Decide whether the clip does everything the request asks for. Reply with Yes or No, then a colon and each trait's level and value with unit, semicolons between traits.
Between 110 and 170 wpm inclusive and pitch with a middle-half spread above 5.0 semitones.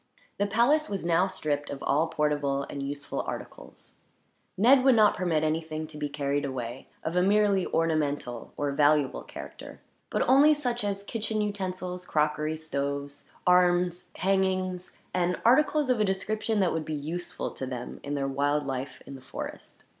Yes: average, 165 wpm; wide, 5.4 semitones